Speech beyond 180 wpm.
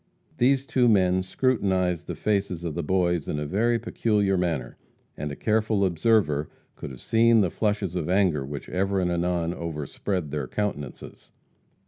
No: average, 160 wpm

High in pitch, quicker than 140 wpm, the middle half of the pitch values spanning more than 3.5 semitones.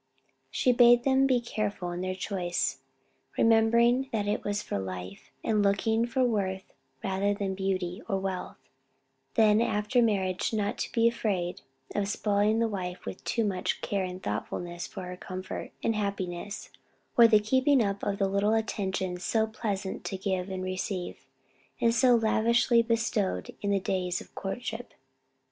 No: high, 205 Hz; average, 160 wpm; average, 3.2 semitones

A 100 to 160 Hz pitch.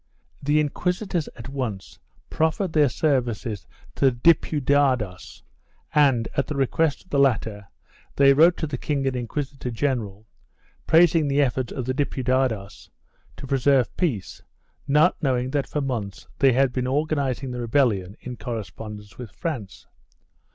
Yes: low, 135 Hz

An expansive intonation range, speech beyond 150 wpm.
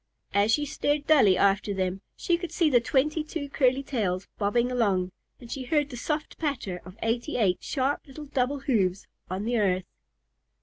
Yes: wide, 6.4 semitones; average, 180 wpm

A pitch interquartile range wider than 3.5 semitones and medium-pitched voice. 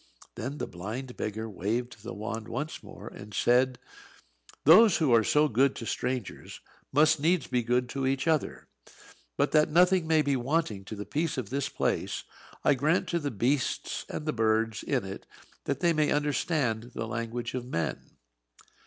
No: average, 5.0 semitones; low, 125 Hz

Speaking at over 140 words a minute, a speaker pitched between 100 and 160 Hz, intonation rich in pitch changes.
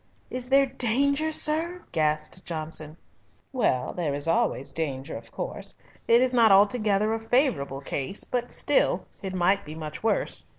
No: average, 155 wpm; high, 205 Hz; wide, 8.2 semitones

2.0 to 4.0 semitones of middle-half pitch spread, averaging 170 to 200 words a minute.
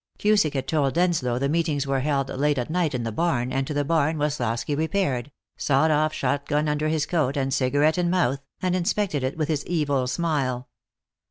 Yes: average, 3.1 semitones; average, 195 wpm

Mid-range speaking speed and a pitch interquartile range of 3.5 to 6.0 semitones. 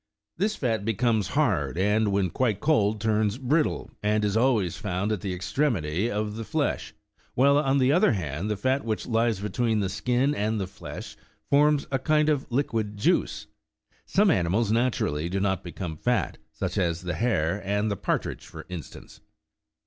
Yes: average, 175 wpm; average, 4.6 semitones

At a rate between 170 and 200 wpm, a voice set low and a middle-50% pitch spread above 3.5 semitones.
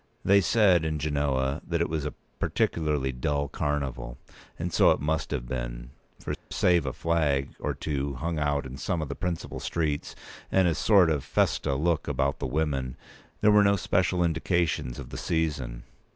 Yes: average, 180 wpm; very low, 75 Hz; average, 3.9 semitones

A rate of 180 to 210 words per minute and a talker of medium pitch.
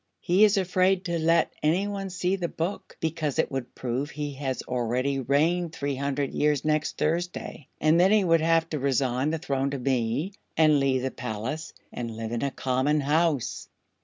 Yes: average, 185 wpm; medium, 150 Hz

